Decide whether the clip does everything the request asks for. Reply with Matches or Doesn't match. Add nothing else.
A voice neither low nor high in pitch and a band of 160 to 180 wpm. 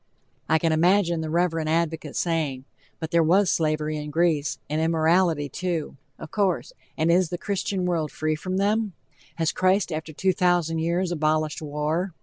Matches